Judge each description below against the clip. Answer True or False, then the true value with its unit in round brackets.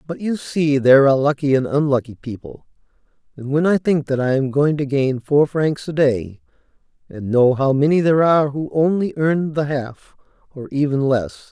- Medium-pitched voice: True (145 Hz)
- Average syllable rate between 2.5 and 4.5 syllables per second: False (5.1 syllables/s)